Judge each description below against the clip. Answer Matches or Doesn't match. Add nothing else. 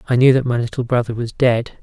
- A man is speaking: Matches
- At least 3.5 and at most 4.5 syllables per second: Doesn't match